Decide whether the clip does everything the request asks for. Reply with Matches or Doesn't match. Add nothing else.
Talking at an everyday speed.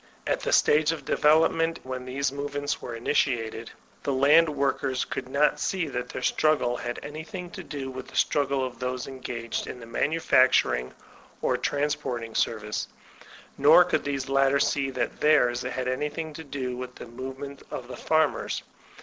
Matches